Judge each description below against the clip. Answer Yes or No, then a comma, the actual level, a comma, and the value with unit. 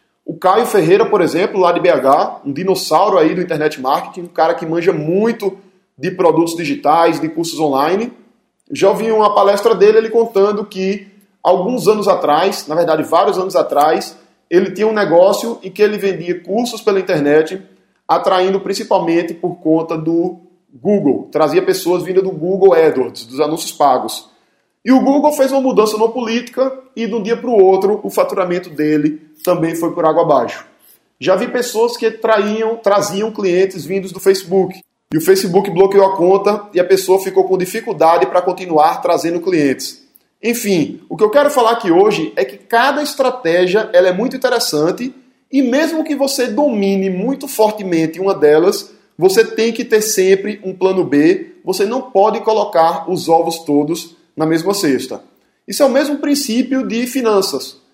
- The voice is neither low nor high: No, high, 195 Hz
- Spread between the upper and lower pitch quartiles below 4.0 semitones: No, average, 4.7 semitones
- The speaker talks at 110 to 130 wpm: No, average, 170 wpm